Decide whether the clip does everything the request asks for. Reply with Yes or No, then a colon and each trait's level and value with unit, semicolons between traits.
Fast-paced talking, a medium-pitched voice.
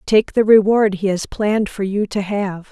No: fast, 220 wpm; high, 205 Hz